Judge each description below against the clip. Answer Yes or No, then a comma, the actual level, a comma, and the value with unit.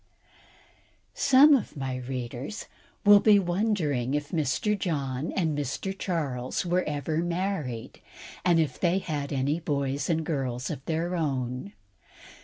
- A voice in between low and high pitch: Yes, medium, 155 Hz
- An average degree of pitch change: Yes, average, 5.0 semitones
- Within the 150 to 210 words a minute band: No, slow, 135 wpm